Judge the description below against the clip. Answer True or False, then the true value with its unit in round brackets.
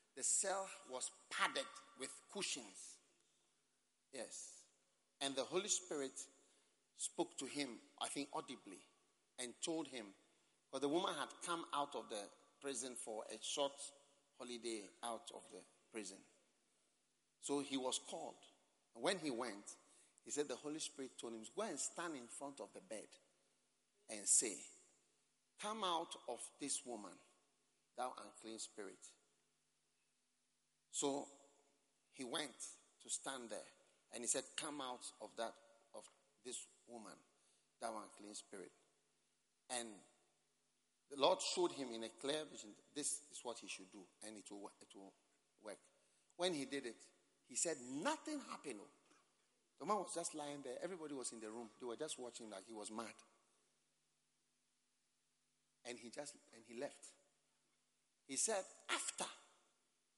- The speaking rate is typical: True (150 wpm)